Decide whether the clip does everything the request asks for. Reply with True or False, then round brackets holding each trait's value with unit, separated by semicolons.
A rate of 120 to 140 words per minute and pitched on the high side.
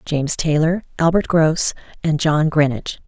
False (135 wpm; 160 Hz)